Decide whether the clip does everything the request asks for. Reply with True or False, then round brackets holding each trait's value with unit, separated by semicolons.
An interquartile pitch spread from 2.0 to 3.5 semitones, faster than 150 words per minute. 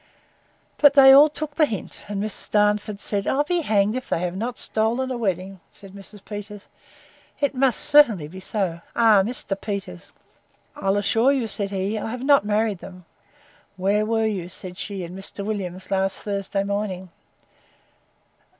True (3.2 semitones; 170 wpm)